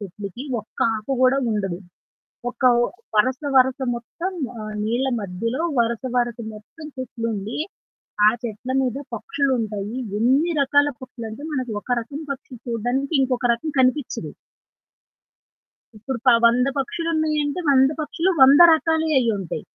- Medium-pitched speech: No, very high, 255 Hz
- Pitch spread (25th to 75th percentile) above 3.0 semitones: Yes, average, 3.7 semitones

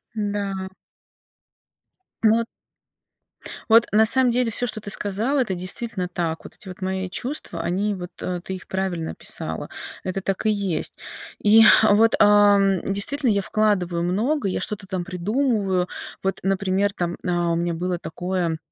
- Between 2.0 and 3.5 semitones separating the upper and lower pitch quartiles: Yes, average, 2.8 semitones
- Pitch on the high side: Yes, high, 195 Hz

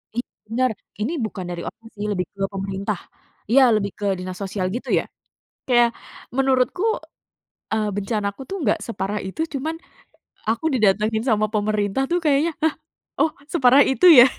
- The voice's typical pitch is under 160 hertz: No, high, 220 Hz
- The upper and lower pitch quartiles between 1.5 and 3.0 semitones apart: No, average, 4.8 semitones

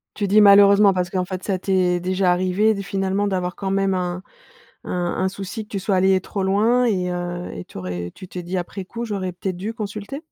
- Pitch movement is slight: Yes, narrow, 1.9 semitones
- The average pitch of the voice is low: No, high, 190 Hz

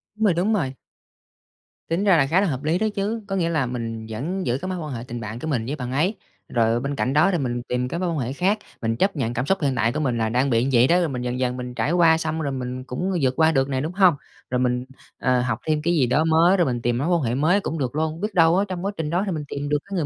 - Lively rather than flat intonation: Yes, wide, 5.7 semitones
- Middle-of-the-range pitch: Yes, medium, 145 Hz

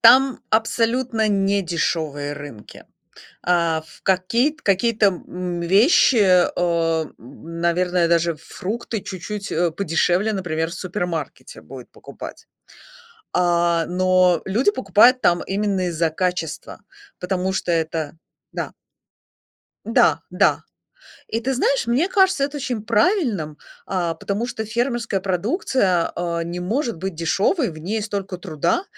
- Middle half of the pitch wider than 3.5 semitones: Yes, average, 4.8 semitones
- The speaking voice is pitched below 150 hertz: No, medium, 185 Hz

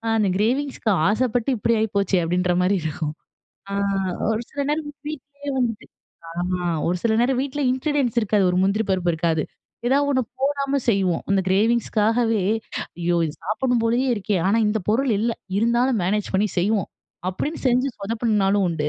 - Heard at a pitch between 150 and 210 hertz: No, high, 220 Hz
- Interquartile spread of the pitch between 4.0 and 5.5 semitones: Yes, average, 4.7 semitones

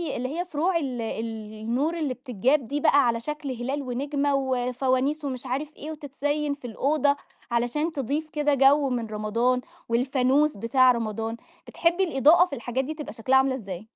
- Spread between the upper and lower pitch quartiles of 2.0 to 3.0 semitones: No, average, 3.4 semitones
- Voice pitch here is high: Yes, very high, 265 Hz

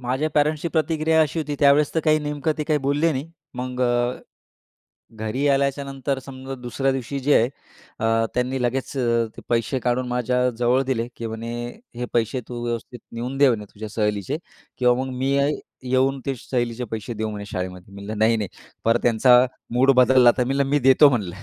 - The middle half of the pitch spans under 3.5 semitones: Yes, average, 3.0 semitones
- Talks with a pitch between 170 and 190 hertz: No, low, 125 Hz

